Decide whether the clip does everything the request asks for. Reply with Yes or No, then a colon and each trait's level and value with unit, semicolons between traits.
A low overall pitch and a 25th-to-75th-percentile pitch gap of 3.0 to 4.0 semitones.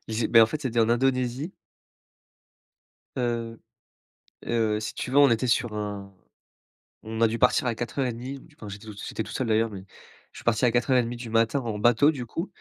No: low, 115 Hz; narrow, 2.4 semitones